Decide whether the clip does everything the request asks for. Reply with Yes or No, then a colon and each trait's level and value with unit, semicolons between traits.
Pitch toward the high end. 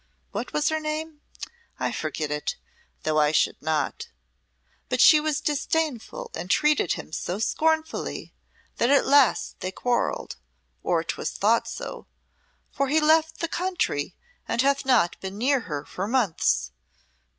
Yes: very high, 265 Hz